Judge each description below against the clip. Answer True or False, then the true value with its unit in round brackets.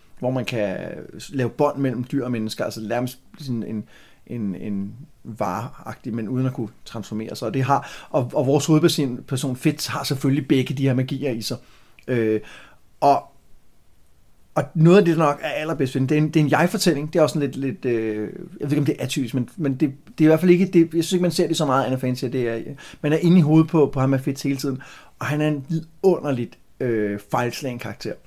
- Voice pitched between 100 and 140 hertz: True (135 Hz)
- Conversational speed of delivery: False (235 wpm)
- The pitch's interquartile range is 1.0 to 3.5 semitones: False (4.0 semitones)